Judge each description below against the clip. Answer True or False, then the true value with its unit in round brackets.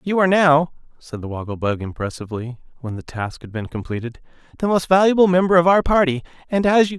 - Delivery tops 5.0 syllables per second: True (6.1 syllables/s)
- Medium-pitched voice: True (150 Hz)